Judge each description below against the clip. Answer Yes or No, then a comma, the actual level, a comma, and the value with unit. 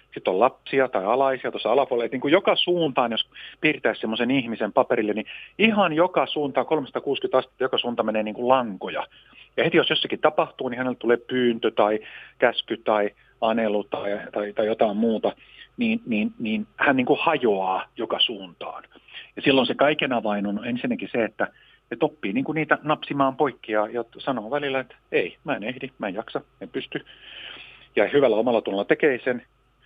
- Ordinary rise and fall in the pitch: No, wide, 5.7 semitones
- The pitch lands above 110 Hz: Yes, low, 130 Hz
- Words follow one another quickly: Yes, fast, 175 wpm